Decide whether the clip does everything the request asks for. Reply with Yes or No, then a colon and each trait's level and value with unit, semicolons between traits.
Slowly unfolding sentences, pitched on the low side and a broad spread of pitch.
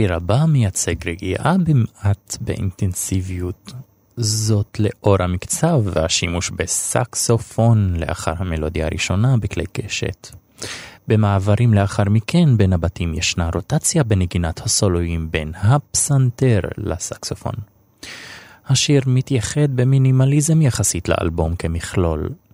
Yes: slow, 90 wpm; low, 100 Hz; wide, 6.0 semitones